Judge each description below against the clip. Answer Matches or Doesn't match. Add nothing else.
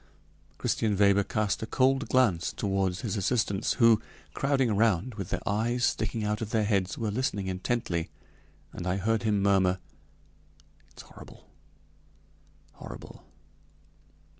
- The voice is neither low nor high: Doesn't match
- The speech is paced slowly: Matches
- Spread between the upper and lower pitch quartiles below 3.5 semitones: Matches